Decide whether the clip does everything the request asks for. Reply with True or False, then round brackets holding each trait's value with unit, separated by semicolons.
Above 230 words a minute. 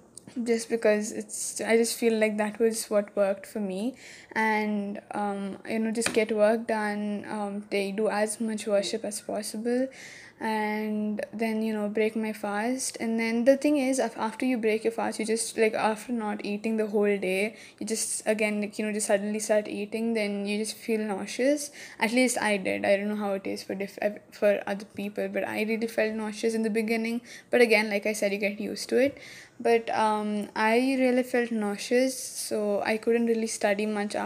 False (205 wpm)